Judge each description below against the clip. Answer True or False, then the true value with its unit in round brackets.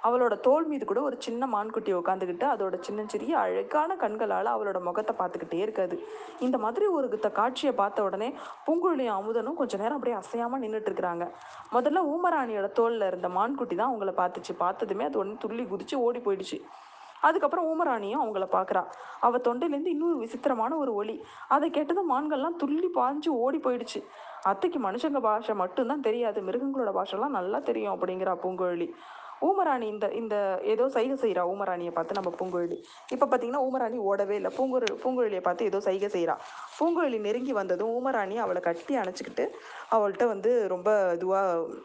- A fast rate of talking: True (150 wpm)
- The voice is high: True (235 Hz)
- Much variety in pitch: True (6.1 semitones)